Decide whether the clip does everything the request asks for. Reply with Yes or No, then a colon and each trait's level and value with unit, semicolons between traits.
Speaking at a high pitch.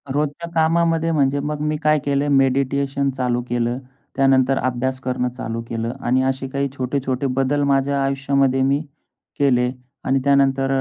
No: low, 135 Hz